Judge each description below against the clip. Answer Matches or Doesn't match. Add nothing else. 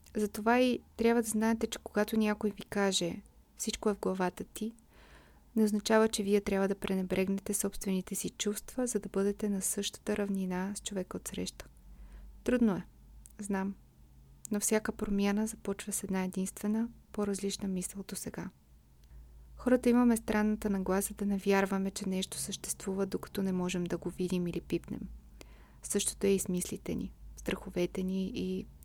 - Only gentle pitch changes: Matches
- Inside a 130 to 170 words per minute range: Matches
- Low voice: Doesn't match